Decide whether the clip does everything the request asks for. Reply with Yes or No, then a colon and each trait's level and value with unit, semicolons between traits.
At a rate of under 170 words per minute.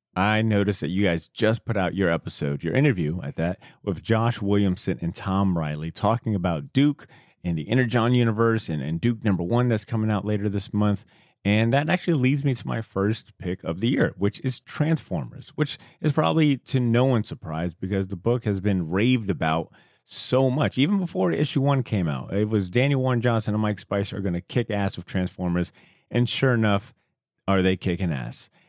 No: fast, 205 wpm